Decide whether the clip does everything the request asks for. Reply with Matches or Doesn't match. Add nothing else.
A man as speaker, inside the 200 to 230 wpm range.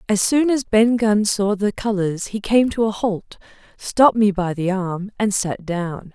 Doesn't match